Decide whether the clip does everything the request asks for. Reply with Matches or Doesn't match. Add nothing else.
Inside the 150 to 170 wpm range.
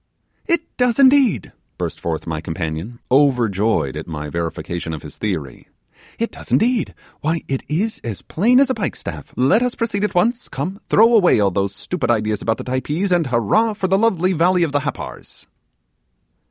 Doesn't match